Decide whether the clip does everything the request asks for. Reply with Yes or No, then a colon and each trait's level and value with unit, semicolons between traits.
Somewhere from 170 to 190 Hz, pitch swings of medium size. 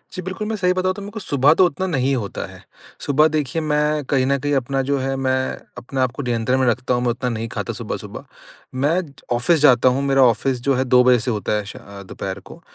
No: low, 135 Hz; average, 3.3 semitones